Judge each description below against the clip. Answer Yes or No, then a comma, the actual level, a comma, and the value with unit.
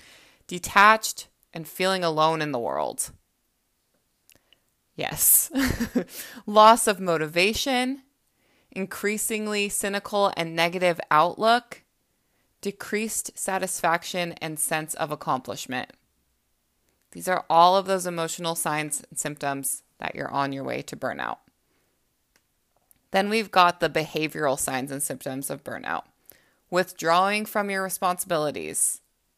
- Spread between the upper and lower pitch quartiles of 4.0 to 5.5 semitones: Yes, average, 4.9 semitones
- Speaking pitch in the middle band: Yes, medium, 175 Hz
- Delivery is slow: Yes, slow, 105 wpm